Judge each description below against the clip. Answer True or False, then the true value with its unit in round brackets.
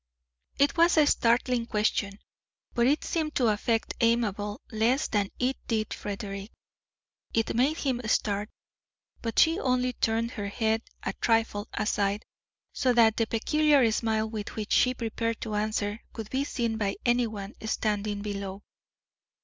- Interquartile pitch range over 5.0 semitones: False (2.8 semitones)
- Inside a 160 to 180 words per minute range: False (145 wpm)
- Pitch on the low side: False (225 Hz)